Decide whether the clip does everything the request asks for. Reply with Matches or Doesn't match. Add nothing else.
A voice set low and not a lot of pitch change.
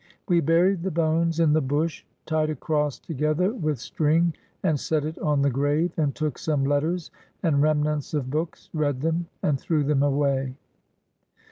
Doesn't match